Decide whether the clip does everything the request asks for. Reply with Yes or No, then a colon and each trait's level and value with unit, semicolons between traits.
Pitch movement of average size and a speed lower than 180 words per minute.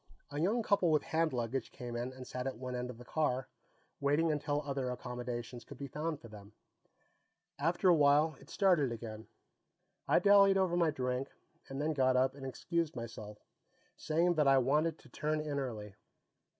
No: average, 4.0 semitones; average, 185 wpm